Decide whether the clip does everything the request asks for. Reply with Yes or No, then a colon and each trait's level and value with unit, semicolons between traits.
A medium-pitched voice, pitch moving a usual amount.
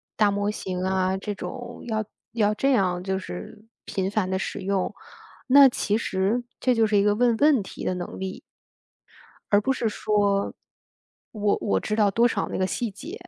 No: high, 205 Hz; average, 3.3 semitones